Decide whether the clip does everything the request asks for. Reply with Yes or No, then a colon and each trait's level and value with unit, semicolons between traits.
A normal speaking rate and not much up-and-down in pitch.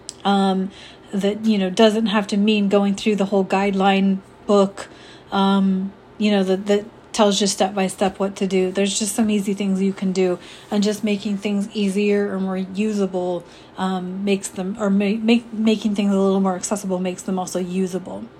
Yes: average, 190 wpm; narrow, 1.4 semitones